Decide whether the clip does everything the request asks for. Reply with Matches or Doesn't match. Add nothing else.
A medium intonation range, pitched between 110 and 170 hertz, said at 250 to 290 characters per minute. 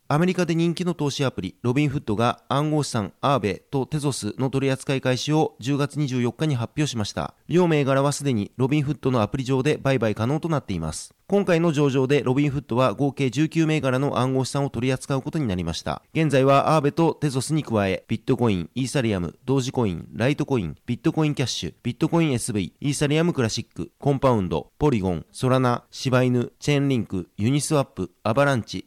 Doesn't match